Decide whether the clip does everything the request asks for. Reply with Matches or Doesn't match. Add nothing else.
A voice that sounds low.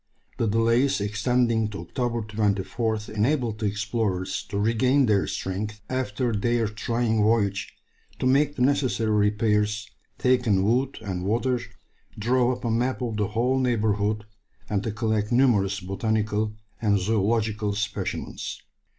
Matches